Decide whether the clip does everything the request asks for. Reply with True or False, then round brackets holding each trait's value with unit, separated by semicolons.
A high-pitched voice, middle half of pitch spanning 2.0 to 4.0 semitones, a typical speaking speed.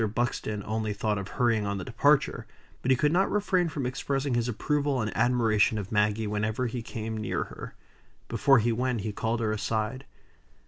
False (115 Hz; 3.2 semitones; 185 wpm)